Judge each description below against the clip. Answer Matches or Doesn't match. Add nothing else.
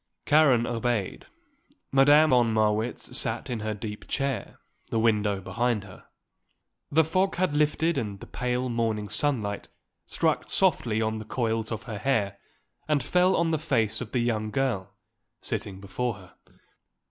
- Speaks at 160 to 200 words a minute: Doesn't match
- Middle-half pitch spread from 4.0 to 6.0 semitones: Matches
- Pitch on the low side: Matches